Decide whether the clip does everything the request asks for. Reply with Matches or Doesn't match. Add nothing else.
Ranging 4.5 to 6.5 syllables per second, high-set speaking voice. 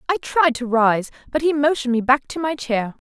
Matches